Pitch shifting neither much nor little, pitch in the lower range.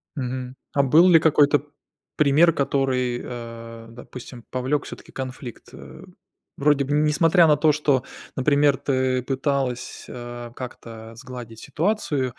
Yes: average, 3.2 semitones; low, 130 Hz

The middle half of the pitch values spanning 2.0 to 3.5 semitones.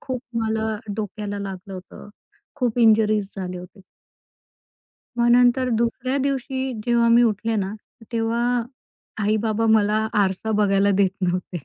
Yes: average, 2.9 semitones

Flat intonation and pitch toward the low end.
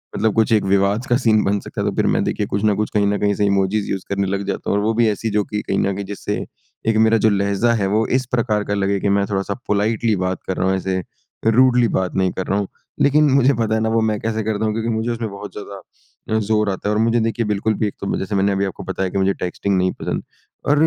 Yes: narrow, 2.1 semitones; low, 105 Hz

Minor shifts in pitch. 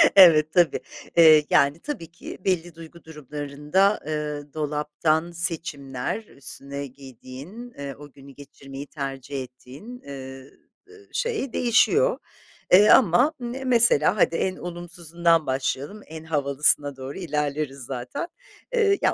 No: average, 4.5 semitones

